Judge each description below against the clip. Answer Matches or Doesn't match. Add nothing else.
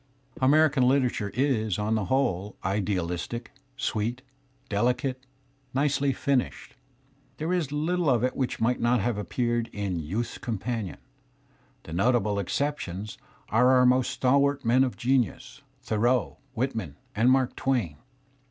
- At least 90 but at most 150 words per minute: Matches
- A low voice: Matches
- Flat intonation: Doesn't match